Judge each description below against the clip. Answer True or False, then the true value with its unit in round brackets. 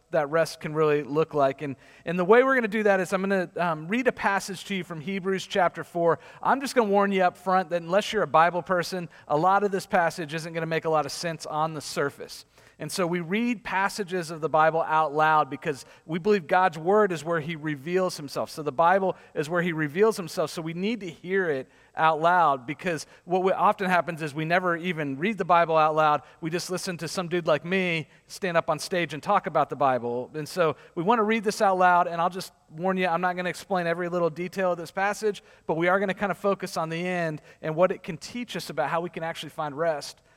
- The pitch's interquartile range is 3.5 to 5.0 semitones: False (3.1 semitones)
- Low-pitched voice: False (175 Hz)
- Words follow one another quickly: True (260 wpm)